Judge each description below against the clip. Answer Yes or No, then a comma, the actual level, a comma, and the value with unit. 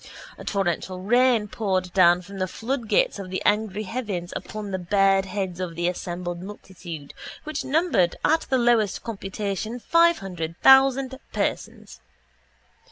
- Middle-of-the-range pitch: No, high, 195 Hz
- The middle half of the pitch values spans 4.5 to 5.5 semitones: Yes, average, 4.9 semitones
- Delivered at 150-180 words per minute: No, average, 140 wpm